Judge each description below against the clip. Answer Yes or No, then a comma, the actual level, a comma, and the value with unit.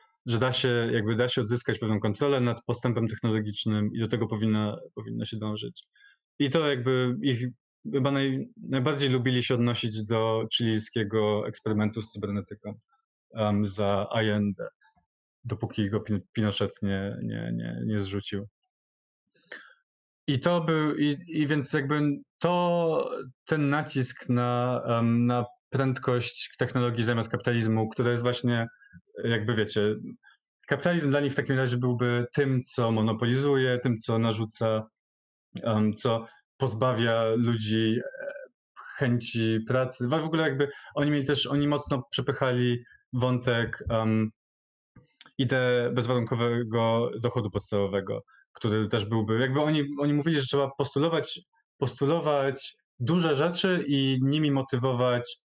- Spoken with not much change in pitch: No, average, 4.1 semitones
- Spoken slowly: No, average, 125 wpm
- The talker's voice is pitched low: Yes, low, 120 Hz